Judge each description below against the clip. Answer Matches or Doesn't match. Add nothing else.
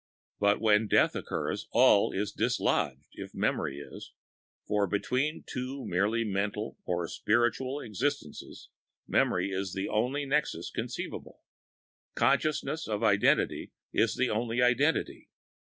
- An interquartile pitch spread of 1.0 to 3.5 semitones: Doesn't match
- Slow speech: Matches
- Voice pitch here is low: Matches